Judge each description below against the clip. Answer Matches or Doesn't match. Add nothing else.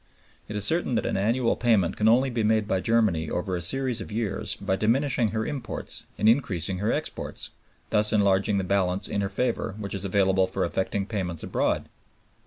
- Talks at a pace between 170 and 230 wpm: Matches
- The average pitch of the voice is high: Doesn't match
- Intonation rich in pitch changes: Doesn't match